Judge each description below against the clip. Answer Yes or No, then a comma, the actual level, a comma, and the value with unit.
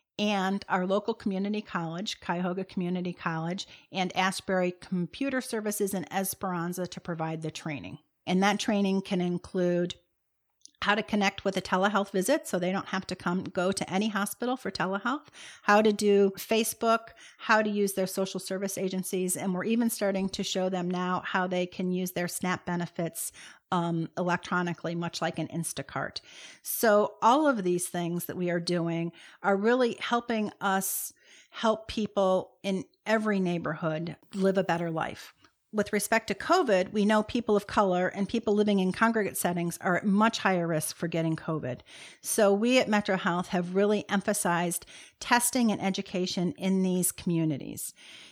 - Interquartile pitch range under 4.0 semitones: Yes, average, 2.7 semitones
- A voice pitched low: No, high, 190 Hz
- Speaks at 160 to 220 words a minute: Yes, average, 165 wpm